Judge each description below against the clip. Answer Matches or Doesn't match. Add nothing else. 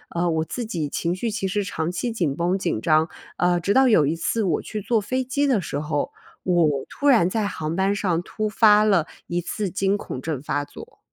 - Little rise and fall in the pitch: Doesn't match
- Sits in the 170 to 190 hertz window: Matches